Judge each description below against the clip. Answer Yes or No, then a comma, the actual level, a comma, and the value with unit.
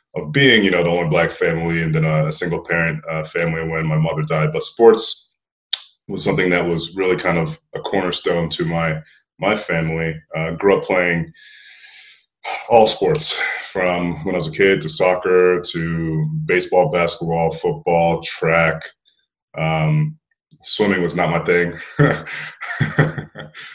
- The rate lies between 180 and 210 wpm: No, average, 150 wpm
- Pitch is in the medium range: No, very low, 85 Hz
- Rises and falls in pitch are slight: Yes, narrow, 1.6 semitones